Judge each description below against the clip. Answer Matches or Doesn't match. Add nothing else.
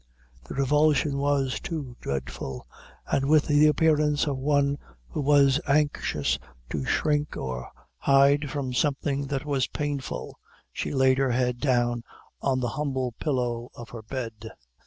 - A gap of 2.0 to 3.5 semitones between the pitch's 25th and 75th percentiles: Matches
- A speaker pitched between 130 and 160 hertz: Matches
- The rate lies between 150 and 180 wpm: Doesn't match